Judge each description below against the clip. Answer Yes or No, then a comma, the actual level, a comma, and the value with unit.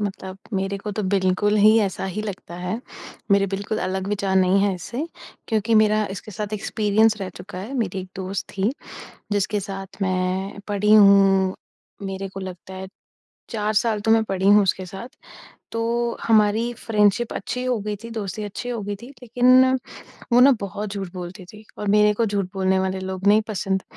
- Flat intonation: Yes, narrow, 2.1 semitones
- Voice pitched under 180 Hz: No, high, 200 Hz